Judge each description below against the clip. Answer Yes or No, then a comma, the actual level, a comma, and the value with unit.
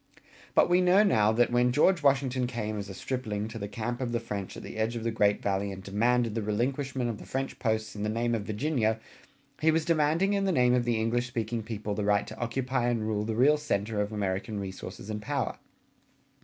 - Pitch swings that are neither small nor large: Yes, average, 3.5 semitones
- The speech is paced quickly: Yes, fast, 230 wpm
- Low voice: Yes, low, 115 Hz